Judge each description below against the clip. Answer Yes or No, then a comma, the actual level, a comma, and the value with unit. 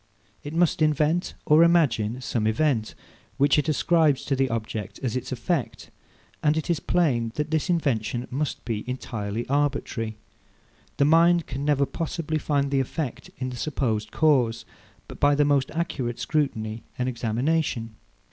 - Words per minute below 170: Yes, average, 150 wpm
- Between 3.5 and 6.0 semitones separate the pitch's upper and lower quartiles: Yes, average, 4.7 semitones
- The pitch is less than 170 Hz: Yes, medium, 140 Hz